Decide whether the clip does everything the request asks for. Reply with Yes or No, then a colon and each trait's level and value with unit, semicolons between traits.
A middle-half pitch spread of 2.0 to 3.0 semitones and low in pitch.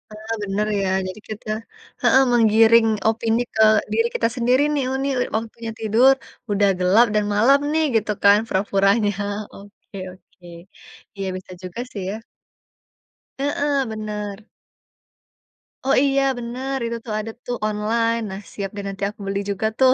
No: narrow, 2.5 semitones; high, 220 Hz